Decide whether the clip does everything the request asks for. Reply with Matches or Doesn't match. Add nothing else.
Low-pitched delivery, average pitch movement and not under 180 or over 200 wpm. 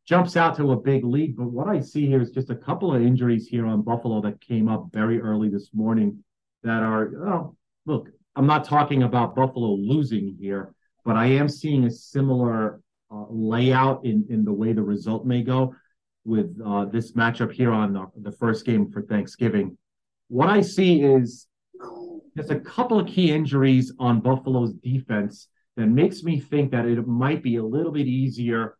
Matches